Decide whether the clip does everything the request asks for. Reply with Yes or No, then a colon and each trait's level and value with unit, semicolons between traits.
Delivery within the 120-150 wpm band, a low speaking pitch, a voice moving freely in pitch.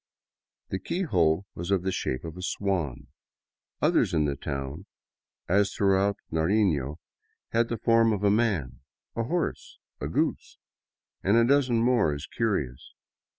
Yes: average, 145 wpm; very low, 95 Hz; wide, 6.3 semitones